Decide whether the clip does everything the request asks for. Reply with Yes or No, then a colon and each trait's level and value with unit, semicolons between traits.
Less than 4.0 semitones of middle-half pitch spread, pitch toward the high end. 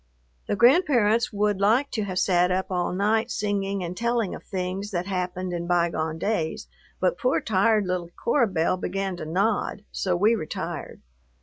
Yes: average, 3.4 semitones; high, 195 Hz